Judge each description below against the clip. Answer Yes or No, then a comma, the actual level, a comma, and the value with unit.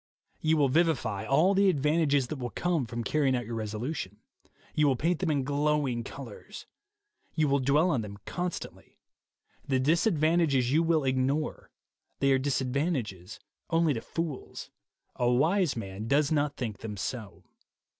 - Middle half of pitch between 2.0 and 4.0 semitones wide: No, average, 4.4 semitones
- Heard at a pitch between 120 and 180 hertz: Yes, medium, 140 Hz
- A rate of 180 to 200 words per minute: No, average, 155 wpm